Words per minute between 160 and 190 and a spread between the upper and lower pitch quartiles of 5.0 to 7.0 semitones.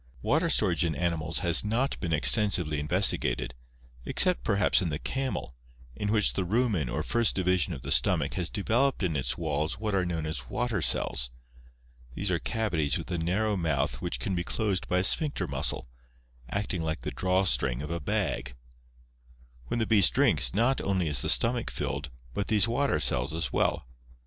Yes: average, 185 wpm; wide, 5.6 semitones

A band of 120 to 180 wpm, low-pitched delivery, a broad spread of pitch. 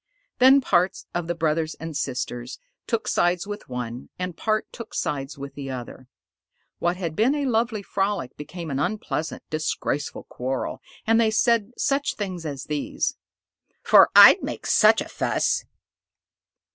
No: average, 150 wpm; medium, 175 Hz; wide, 7.4 semitones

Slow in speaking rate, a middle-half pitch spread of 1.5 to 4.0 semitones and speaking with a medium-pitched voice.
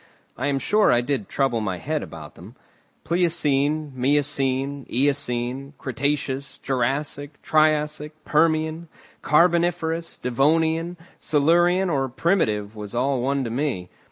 Yes: slow, 115 wpm; average, 3.3 semitones; medium, 145 Hz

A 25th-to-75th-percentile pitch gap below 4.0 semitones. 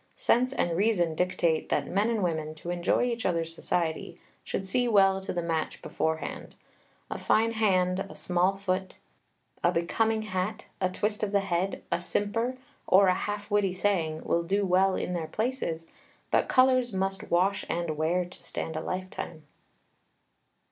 Yes: average, 3.2 semitones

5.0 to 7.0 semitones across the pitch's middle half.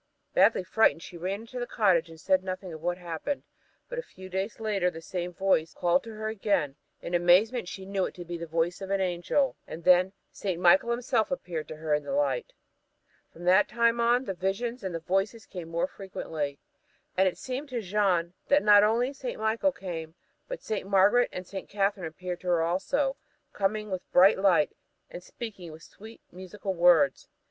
No: average, 3.9 semitones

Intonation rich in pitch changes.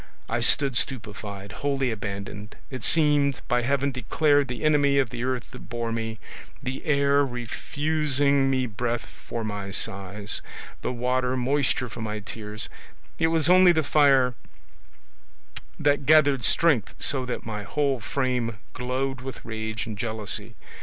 No: average, 4.0 semitones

